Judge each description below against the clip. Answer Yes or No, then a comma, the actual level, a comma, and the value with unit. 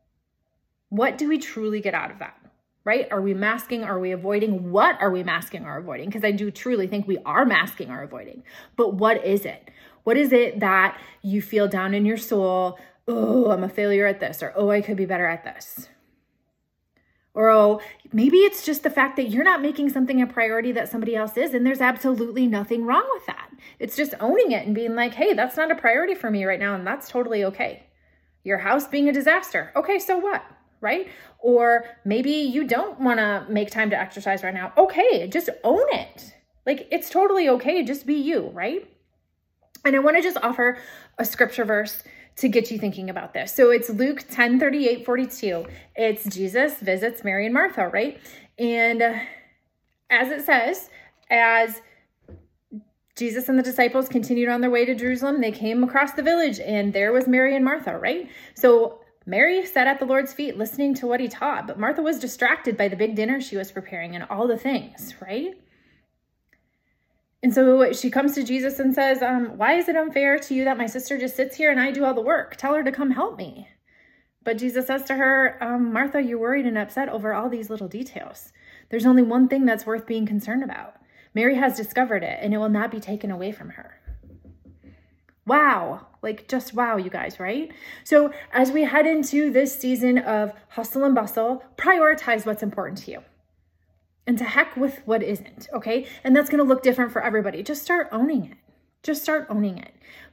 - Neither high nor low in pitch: No, high, 245 Hz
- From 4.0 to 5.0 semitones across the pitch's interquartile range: Yes, average, 4.3 semitones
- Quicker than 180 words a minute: Yes, average, 200 wpm